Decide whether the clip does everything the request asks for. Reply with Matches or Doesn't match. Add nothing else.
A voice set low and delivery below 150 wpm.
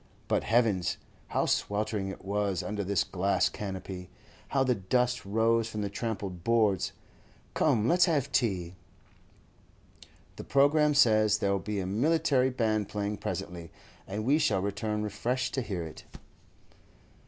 Matches